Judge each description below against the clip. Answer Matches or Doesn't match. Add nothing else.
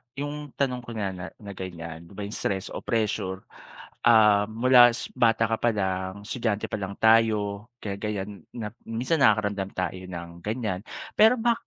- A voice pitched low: Matches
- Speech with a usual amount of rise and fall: Matches